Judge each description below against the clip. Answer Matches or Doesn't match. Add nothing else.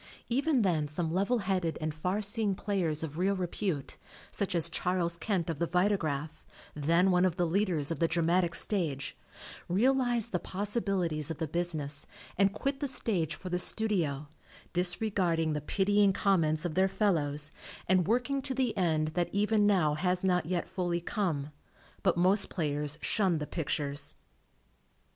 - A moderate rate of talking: Matches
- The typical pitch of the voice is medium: Matches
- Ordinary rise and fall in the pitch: Matches